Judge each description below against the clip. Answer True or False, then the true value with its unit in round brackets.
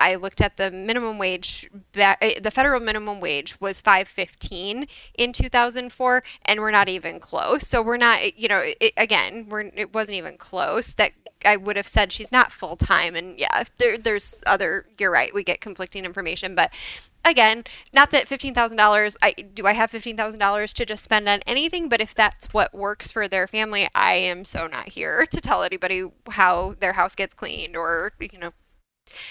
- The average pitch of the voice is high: True (210 Hz)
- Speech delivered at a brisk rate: False (185 wpm)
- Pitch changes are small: False (3.4 semitones)